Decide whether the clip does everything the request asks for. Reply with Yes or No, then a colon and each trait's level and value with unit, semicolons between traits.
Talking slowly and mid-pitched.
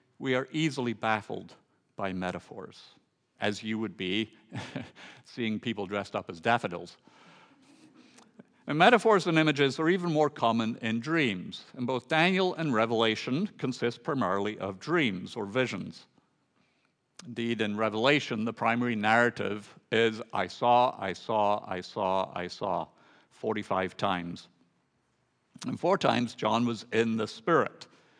No: slow, 130 wpm; low, 115 Hz